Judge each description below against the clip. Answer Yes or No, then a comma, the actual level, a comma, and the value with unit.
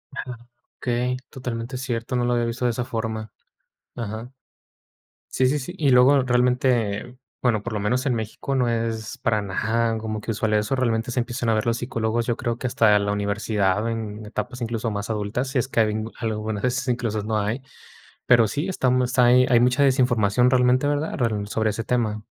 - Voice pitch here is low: Yes, low, 115 Hz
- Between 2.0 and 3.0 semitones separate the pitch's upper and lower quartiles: Yes, narrow, 2.4 semitones